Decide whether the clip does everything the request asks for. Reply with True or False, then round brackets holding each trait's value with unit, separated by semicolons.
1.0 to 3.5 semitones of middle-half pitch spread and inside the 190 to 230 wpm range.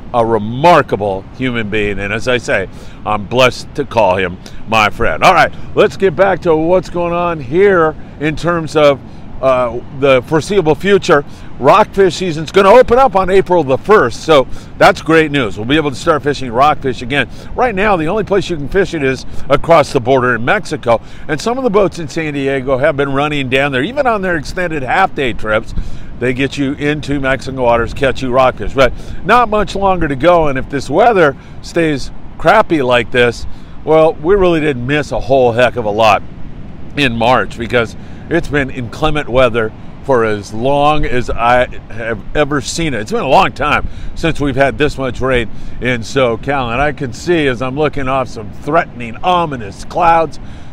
False (5.0 semitones; 195 wpm)